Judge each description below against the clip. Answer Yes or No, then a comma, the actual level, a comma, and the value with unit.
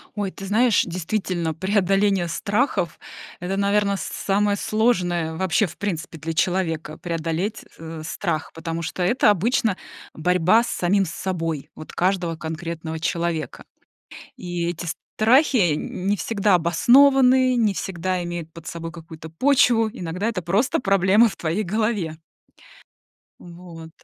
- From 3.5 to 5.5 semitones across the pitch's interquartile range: Yes, average, 3.8 semitones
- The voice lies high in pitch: No, medium, 180 Hz